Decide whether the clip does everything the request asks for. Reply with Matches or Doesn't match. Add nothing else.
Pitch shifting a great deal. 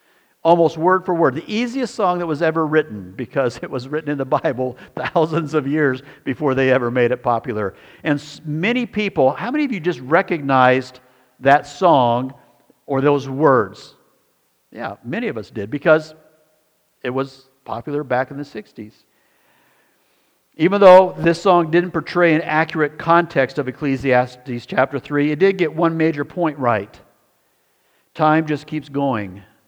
Doesn't match